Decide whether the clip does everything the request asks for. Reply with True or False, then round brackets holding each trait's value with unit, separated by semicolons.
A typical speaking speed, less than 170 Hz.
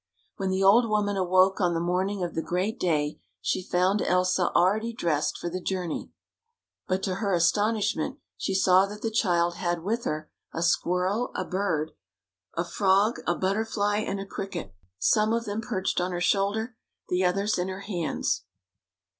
False (175 wpm; 190 Hz)